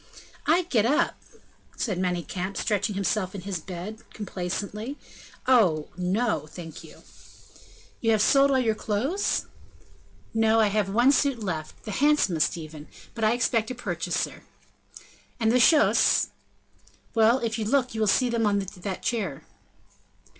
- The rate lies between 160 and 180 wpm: No, average, 145 wpm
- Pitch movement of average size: Yes, average, 4.4 semitones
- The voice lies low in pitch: No, high, 215 Hz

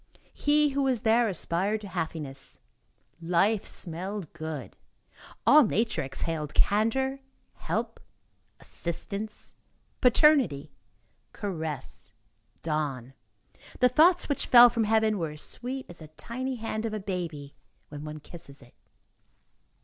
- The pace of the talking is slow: Yes, slow, 120 wpm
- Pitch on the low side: No, high, 200 Hz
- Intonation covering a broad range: Yes, wide, 7.2 semitones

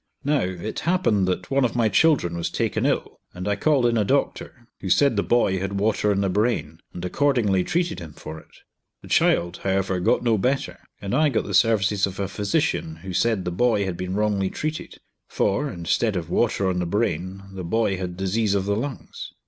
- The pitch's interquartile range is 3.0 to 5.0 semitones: Yes, average, 4.3 semitones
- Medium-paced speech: No, fast, 210 wpm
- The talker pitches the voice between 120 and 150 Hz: No, low, 100 Hz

